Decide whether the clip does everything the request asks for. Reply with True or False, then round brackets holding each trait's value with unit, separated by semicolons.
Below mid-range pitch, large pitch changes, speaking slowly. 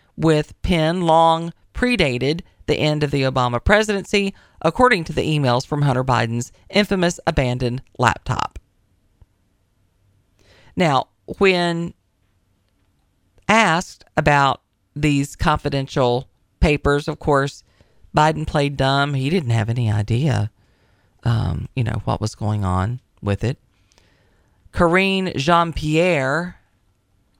True (130 Hz; 7.8 semitones; 105 wpm)